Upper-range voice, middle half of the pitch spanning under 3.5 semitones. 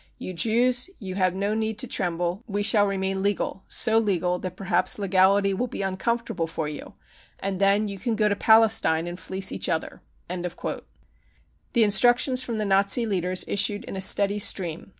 Yes: high, 195 Hz; average, 2.9 semitones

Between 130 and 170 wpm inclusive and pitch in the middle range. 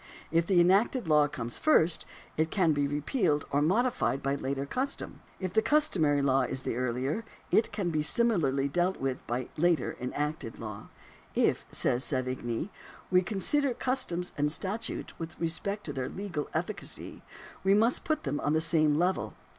No: average, 180 wpm; medium, 160 Hz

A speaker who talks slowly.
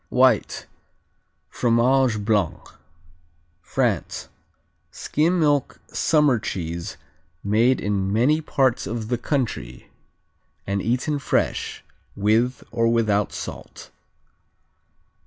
Yes: slow, 85 wpm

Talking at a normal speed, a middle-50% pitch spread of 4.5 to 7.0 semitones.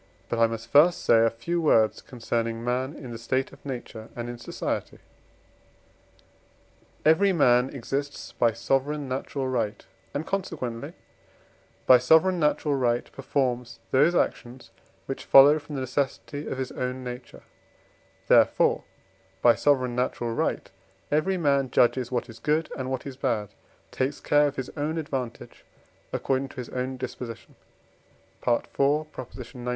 No: average, 145 wpm; average, 3.2 semitones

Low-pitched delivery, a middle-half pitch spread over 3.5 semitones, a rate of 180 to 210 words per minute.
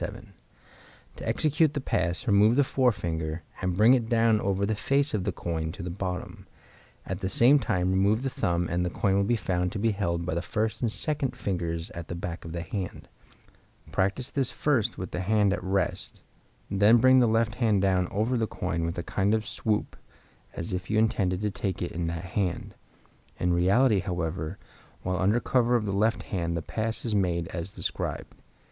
Yes: low, 100 Hz; average, 4.2 semitones; fast, 205 wpm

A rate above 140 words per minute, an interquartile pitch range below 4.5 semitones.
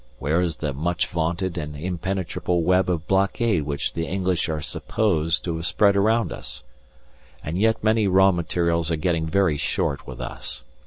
Yes: average, 170 wpm; average, 3.1 semitones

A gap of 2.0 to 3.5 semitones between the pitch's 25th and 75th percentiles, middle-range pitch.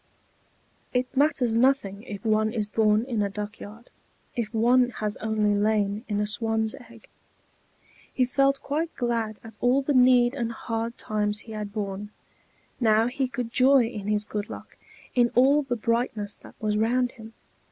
No: average, 2.8 semitones; high, 225 Hz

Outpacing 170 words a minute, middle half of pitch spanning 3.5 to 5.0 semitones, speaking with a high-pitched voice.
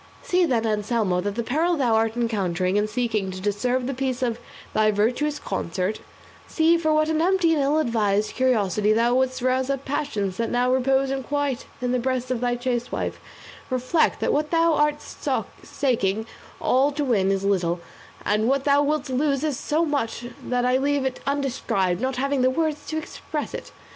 Yes: average, 185 wpm; average, 4.7 semitones; very high, 255 Hz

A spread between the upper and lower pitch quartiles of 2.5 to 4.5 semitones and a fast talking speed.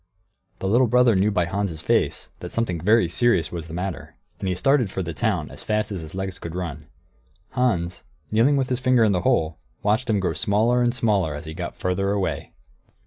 No: average, 4.9 semitones; fast, 210 wpm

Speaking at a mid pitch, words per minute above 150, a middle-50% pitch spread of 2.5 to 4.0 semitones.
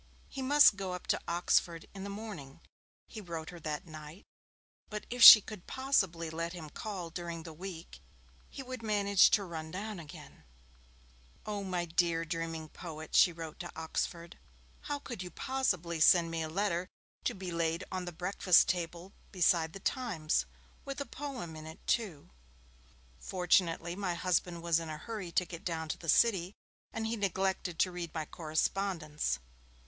Yes: medium, 175 Hz; average, 170 wpm; average, 3.4 semitones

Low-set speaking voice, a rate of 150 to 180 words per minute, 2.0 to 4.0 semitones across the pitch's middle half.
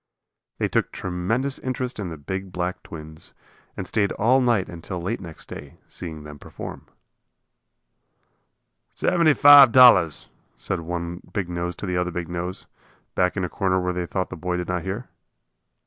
Yes: very low, 90 Hz; average, 170 wpm; average, 3.3 semitones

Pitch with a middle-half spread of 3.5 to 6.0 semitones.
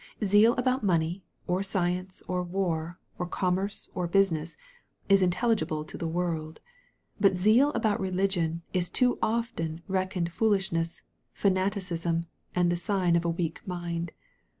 No: average, 2.7 semitones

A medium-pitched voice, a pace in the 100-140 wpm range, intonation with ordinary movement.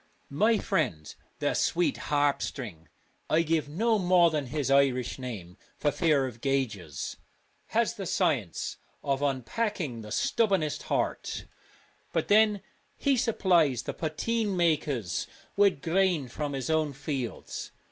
No: medium, 150 Hz; slow, 135 wpm; wide, 6.1 semitones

